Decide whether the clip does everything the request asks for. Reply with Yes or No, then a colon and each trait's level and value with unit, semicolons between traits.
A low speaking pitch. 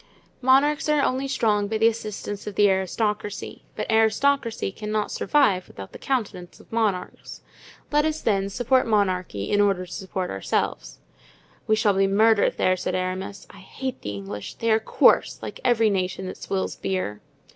No: high, 205 Hz